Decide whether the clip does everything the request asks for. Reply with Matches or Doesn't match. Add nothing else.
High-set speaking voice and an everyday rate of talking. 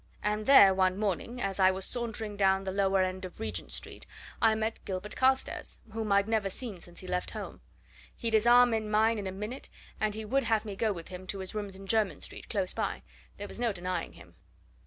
Doesn't match